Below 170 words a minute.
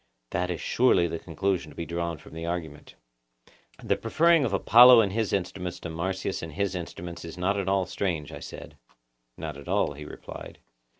No: average, 190 wpm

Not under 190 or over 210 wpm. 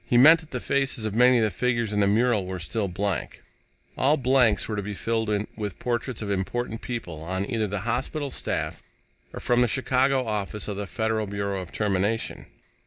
Yes: average, 200 wpm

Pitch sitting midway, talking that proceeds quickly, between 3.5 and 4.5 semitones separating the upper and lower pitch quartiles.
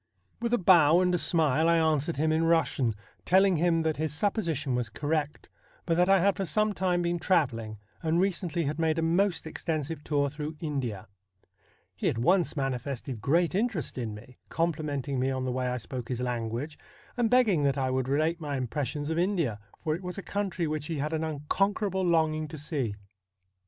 Yes: medium, 155 Hz; fast, 210 wpm; average, 4.2 semitones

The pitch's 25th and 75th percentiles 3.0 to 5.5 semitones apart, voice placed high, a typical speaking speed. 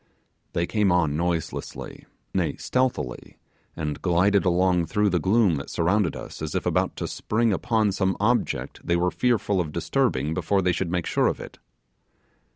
No: average, 3.5 semitones; very low, 90 Hz; average, 165 wpm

